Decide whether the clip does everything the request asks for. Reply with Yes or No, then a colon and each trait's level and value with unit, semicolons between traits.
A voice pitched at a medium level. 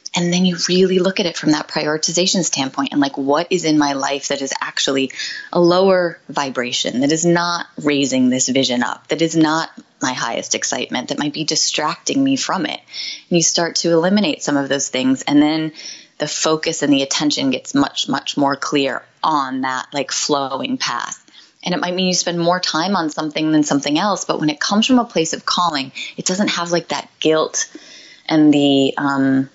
Yes: medium, 155 Hz